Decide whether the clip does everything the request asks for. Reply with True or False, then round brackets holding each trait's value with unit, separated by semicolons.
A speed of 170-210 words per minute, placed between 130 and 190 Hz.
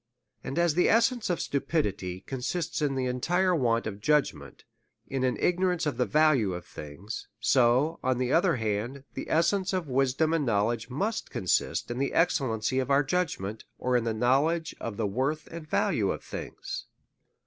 True (180 wpm; 135 Hz)